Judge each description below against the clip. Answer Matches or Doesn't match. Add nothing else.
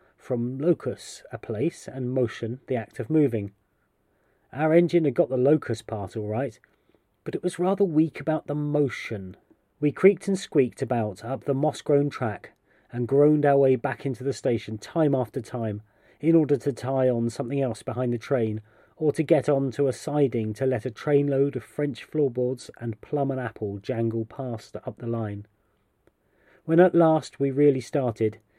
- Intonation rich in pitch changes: Doesn't match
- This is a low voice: Matches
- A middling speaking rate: Matches